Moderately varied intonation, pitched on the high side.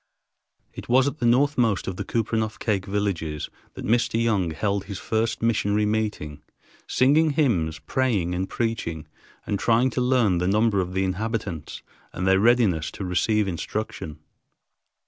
No: average, 4.0 semitones; low, 105 Hz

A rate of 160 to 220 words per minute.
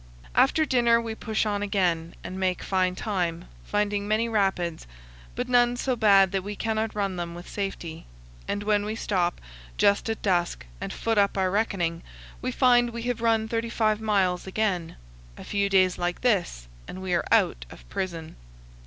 Yes: average, 175 wpm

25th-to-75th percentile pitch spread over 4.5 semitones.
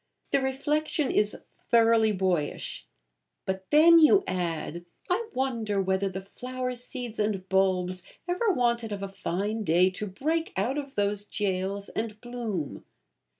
Yes: average, 5.1 semitones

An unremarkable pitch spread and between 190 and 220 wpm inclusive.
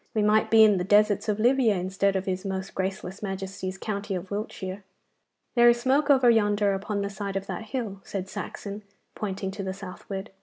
No: narrow, 2.0 semitones; average, 195 wpm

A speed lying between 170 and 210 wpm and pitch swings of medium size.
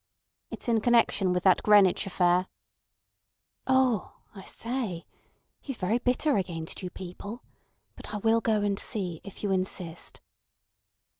No: slow, 135 wpm; average, 4.0 semitones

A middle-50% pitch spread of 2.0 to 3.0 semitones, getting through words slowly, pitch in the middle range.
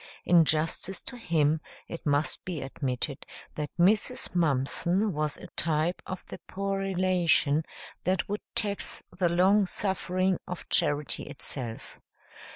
No: average, 4.0 semitones; slow, 130 wpm; medium, 175 Hz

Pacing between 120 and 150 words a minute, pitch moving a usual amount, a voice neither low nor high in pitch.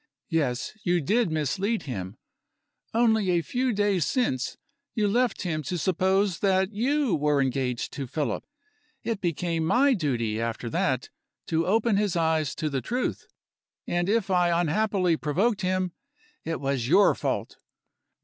No: average, 145 wpm; wide, 5.8 semitones; medium, 175 Hz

